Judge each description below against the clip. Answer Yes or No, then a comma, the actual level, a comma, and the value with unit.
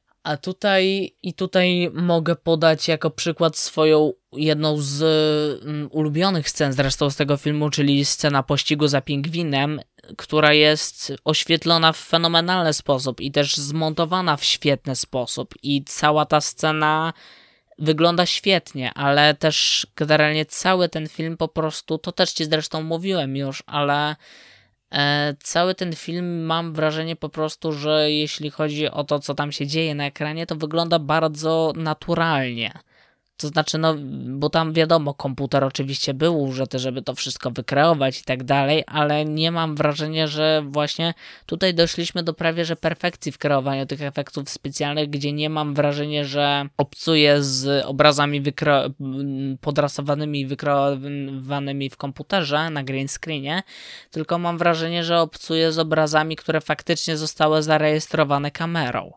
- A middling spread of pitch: No, narrow, 2.3 semitones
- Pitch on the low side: No, medium, 150 Hz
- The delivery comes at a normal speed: Yes, average, 140 wpm